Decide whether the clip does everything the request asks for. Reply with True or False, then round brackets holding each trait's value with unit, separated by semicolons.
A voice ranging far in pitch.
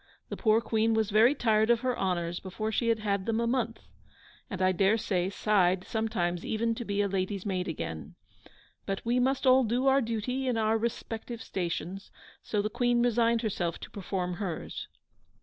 False (3.5 semitones)